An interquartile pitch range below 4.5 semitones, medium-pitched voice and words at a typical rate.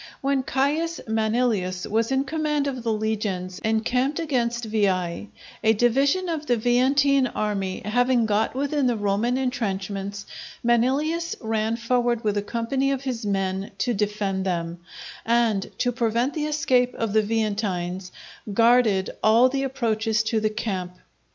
No: average, 3.9 semitones; high, 230 Hz; average, 145 wpm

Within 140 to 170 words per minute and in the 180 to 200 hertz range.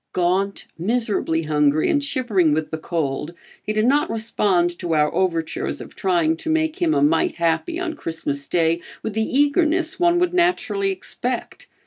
Yes: average, 165 wpm; high, 190 Hz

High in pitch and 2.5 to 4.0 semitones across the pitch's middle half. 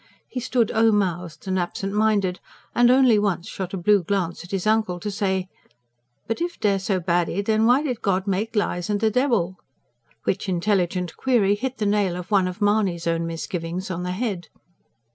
Yes: high, 195 Hz; average, 3.3 semitones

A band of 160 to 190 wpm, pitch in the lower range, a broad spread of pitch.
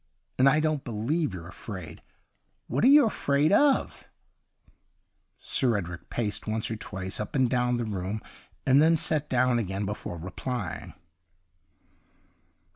No: average, 140 wpm; low, 120 Hz; wide, 6.0 semitones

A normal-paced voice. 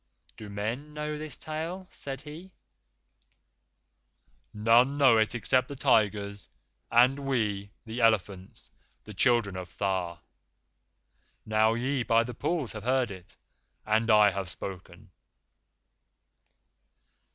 No: slow, 115 wpm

